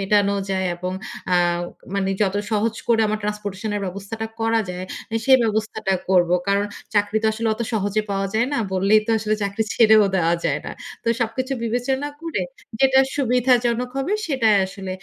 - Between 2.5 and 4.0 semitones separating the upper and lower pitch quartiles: Yes, average, 2.9 semitones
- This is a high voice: Yes, high, 215 Hz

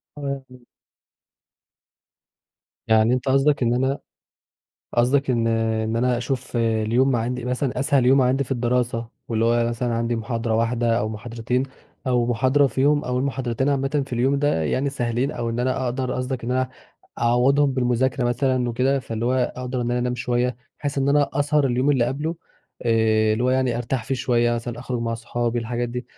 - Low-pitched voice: Yes, low, 125 Hz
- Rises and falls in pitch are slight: Yes, narrow, 2.0 semitones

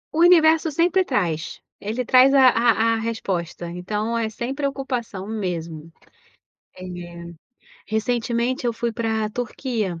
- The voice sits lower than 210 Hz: No, high, 230 Hz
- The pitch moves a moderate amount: Yes, average, 4.2 semitones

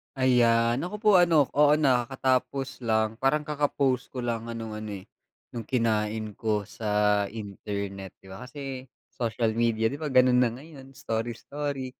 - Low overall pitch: Yes, low, 120 Hz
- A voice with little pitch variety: No, average, 3.6 semitones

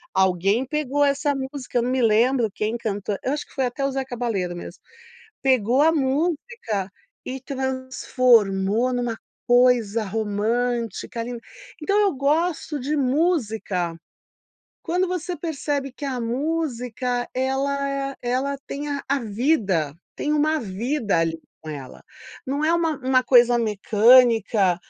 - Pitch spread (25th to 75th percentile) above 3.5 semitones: Yes, average, 4.1 semitones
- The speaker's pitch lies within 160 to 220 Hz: No, very high, 255 Hz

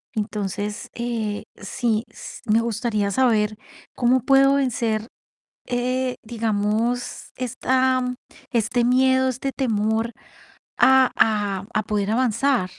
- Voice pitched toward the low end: No, high, 230 Hz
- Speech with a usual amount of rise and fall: Yes, average, 3.2 semitones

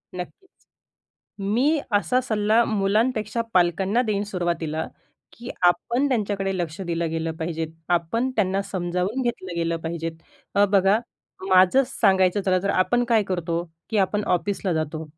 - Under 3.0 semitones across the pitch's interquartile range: No, average, 3.9 semitones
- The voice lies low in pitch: No, high, 195 Hz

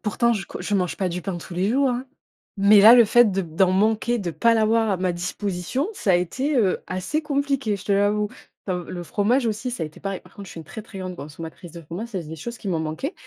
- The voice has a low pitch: No, high, 200 Hz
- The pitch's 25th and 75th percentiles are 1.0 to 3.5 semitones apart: No, average, 4.5 semitones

